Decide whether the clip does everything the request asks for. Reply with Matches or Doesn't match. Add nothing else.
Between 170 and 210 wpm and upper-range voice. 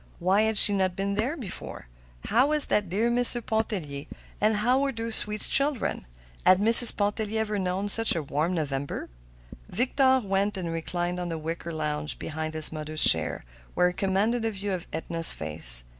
Matches